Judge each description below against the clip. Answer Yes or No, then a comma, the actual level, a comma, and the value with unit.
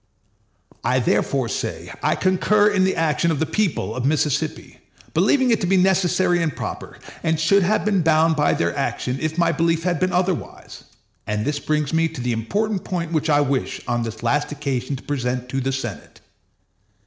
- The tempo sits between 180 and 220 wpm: Yes, average, 190 wpm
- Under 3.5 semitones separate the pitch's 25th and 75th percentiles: No, average, 5.0 semitones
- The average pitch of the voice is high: No, medium, 160 Hz